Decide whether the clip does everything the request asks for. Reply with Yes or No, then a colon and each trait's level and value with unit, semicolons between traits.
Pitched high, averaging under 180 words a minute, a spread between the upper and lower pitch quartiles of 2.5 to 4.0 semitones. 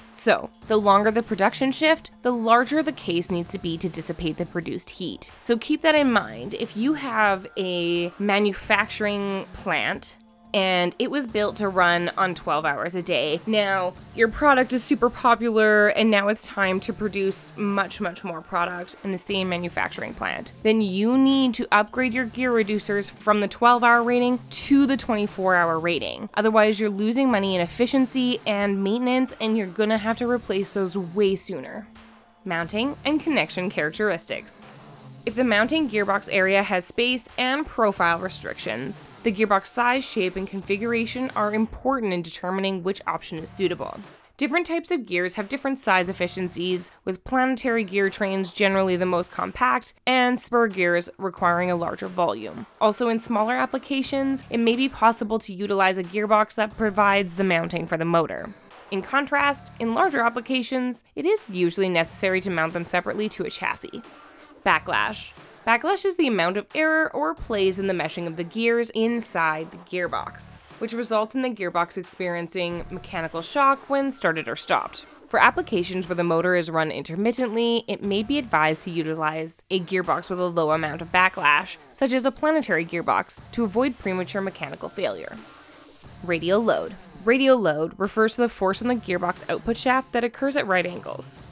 No: high, 205 Hz; average, 170 wpm; average, 4.8 semitones